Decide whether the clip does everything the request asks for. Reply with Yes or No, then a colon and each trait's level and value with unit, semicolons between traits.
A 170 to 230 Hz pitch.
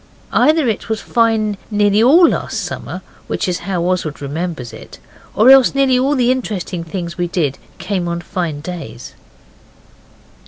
Yes: high, 190 Hz